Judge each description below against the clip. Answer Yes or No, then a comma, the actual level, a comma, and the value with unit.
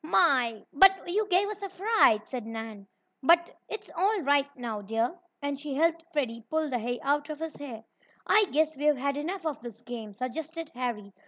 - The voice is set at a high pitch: Yes, very high, 285 Hz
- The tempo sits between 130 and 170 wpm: No, average, 190 wpm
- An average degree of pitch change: No, wide, 5.7 semitones